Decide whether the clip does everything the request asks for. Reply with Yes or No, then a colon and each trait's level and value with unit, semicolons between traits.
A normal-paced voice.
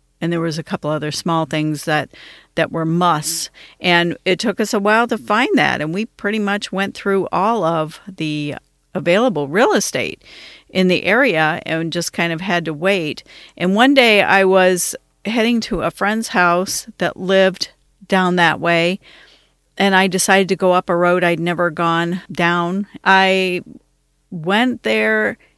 Yes: average, 170 wpm